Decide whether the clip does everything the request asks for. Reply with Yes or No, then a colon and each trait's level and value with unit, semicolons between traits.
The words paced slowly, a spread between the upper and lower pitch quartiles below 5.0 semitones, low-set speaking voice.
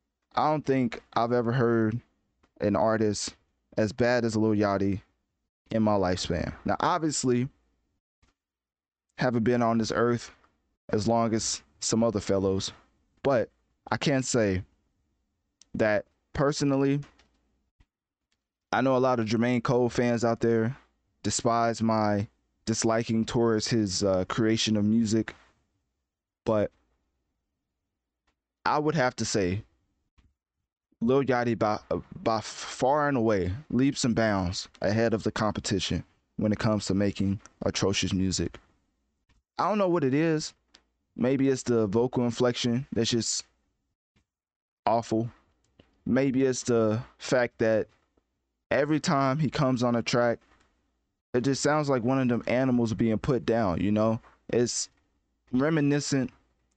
Yes: slow, 130 wpm; average, 4.1 semitones; low, 115 Hz